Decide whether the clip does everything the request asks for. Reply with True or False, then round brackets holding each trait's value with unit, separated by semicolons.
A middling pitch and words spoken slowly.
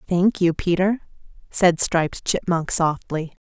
True (175 Hz; 120 wpm)